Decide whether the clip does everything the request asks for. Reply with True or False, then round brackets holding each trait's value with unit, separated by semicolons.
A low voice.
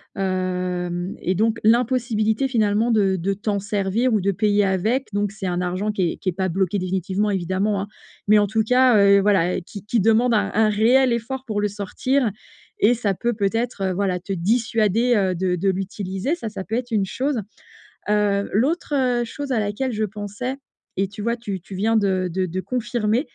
False (205 Hz)